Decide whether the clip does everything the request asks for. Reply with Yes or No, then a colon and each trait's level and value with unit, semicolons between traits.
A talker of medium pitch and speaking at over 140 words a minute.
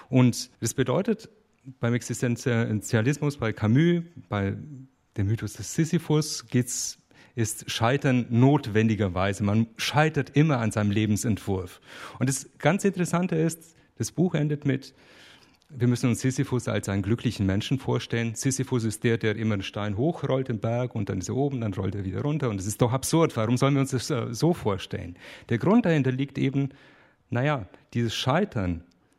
No: low, 125 Hz; average, 165 wpm